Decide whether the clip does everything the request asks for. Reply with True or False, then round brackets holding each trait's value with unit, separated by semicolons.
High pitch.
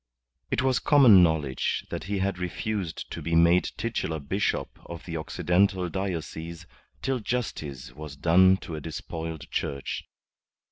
False (85 Hz)